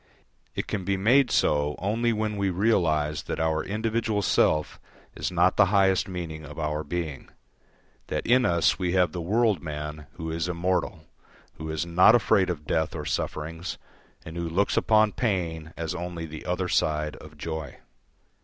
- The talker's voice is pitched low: Yes, very low, 85 Hz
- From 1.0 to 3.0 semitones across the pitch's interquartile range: No, average, 4.0 semitones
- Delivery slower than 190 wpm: Yes, average, 170 wpm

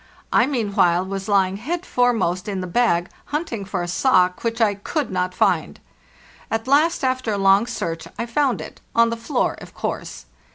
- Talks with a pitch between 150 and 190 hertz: No, high, 215 Hz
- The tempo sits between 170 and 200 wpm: Yes, average, 175 wpm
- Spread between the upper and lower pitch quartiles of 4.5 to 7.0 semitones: Yes, average, 4.9 semitones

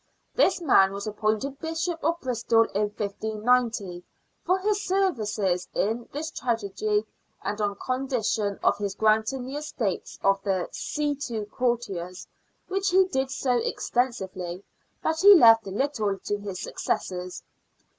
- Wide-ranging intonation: Yes, wide, 5.7 semitones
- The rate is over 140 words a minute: No, slow, 135 wpm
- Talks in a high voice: Yes, high, 225 Hz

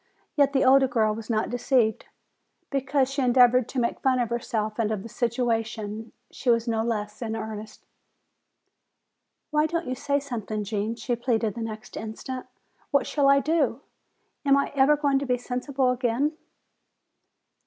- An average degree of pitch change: Yes, average, 3.5 semitones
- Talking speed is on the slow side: No, average, 165 wpm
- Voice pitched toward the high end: Yes, high, 245 Hz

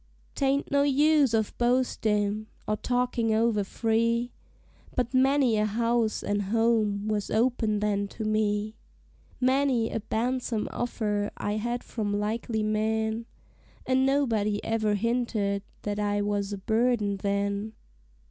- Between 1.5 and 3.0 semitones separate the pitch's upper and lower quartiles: Yes, narrow, 2.6 semitones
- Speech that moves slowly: Yes, slow, 130 wpm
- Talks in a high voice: Yes, high, 220 Hz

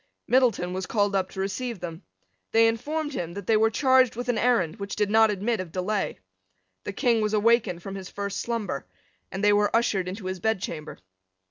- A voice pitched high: Yes, high, 210 Hz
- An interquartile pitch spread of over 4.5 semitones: No, average, 3.4 semitones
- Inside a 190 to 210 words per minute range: Yes, average, 200 wpm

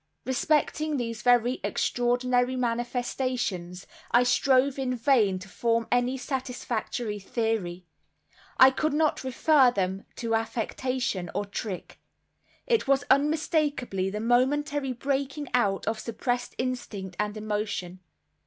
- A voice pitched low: No, high, 245 Hz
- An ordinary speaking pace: No, slow, 110 wpm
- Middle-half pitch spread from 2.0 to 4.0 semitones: Yes, average, 3.7 semitones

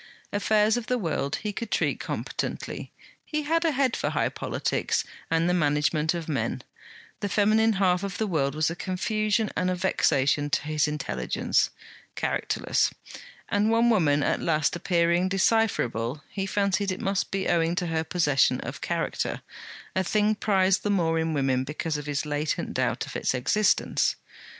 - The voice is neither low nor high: Yes, medium, 180 Hz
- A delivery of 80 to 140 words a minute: No, average, 170 wpm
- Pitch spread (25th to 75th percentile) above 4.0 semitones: Yes, average, 5.3 semitones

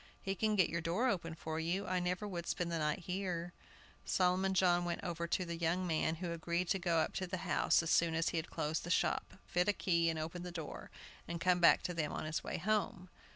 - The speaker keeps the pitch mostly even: Yes, narrow, 1.8 semitones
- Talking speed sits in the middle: No, fast, 245 wpm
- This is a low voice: No, medium, 175 Hz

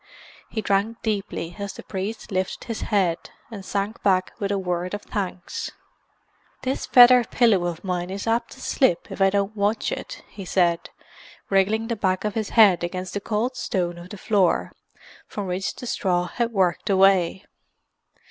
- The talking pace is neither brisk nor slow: Yes, average, 175 wpm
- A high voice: Yes, high, 195 Hz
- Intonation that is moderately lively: Yes, average, 3.0 semitones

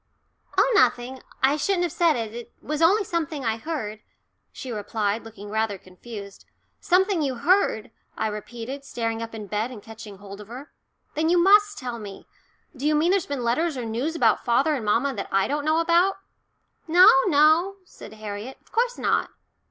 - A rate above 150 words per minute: Yes, average, 185 wpm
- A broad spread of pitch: Yes, wide, 6.9 semitones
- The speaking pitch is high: Yes, very high, 255 Hz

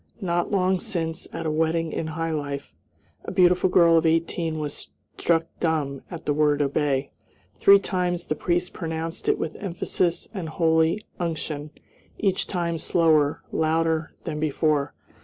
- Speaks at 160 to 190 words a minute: No, average, 150 wpm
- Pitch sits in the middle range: Yes, medium, 165 Hz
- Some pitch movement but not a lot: No, narrow, 2.1 semitones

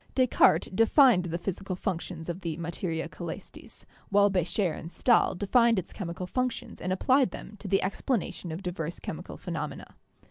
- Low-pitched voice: No, medium, 185 Hz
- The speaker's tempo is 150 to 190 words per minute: Yes, average, 155 wpm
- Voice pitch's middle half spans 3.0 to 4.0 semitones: Yes, average, 3.4 semitones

